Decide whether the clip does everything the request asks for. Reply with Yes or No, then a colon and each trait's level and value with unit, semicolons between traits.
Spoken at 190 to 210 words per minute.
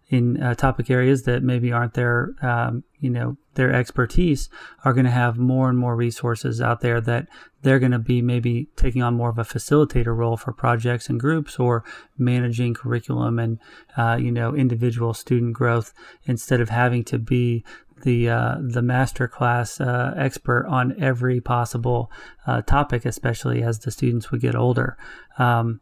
No: average, 175 wpm